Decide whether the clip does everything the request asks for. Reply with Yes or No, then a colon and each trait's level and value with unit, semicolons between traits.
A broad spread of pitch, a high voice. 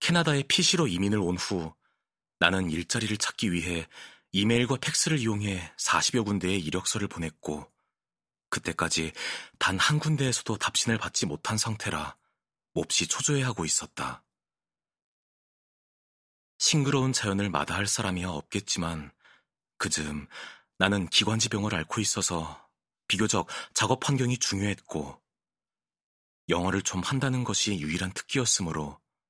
No: wide, 6.0 semitones; low, 100 Hz